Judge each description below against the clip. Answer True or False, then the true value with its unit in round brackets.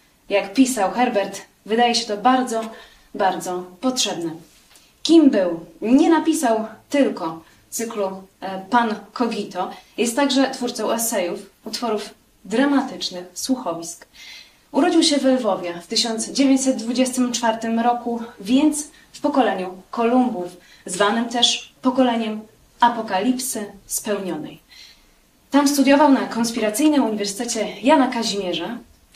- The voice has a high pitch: True (230 Hz)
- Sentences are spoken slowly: True (95 wpm)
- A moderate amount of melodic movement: True (4.7 semitones)